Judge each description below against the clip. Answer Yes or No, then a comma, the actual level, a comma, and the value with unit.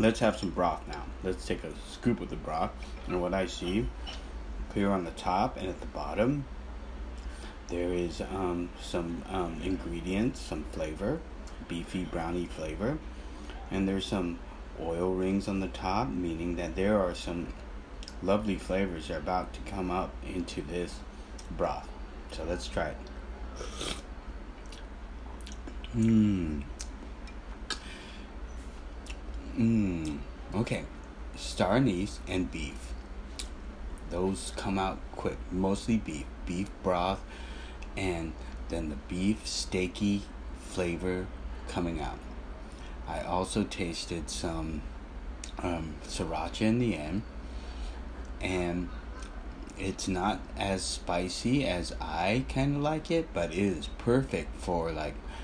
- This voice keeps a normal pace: No, slow, 120 wpm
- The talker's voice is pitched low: Yes, very low, 80 Hz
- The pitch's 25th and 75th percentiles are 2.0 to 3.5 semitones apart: No, average, 5.3 semitones